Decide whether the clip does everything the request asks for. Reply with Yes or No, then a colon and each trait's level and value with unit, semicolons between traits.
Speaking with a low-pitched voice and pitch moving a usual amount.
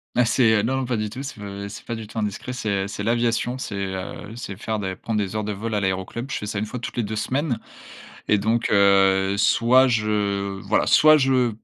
Yes: low, 110 Hz; average, 3.2 semitones